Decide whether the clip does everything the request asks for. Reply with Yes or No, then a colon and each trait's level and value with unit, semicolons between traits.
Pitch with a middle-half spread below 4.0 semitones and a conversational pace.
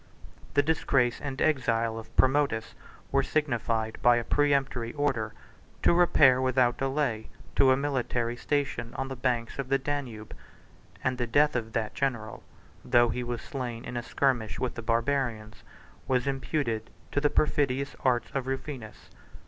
Yes: average, 3.0 semitones; average, 155 wpm